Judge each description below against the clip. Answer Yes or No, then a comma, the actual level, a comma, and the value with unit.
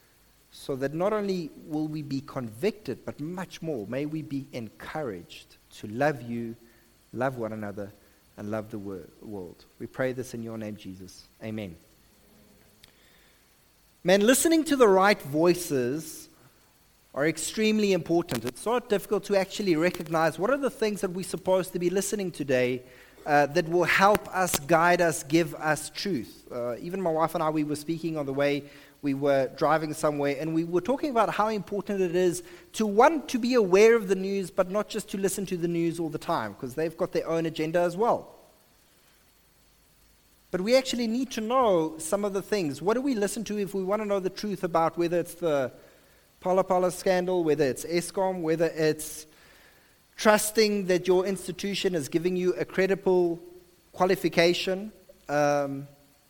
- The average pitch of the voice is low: No, medium, 170 Hz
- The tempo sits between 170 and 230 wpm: Yes, average, 175 wpm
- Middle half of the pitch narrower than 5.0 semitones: No, average, 5.3 semitones